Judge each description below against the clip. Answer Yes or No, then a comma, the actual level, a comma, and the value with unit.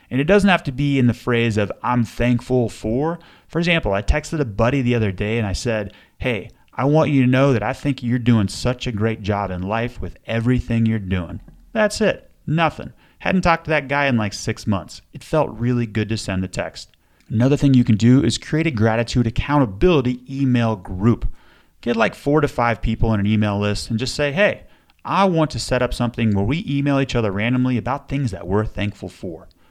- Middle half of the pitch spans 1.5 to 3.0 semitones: No, average, 4.6 semitones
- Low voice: Yes, low, 120 Hz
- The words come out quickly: Yes, fast, 220 wpm